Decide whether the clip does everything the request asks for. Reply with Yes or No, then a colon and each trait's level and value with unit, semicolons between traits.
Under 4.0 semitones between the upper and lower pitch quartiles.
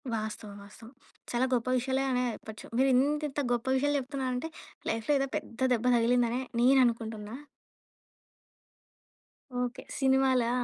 Yes: narrow, 2.5 semitones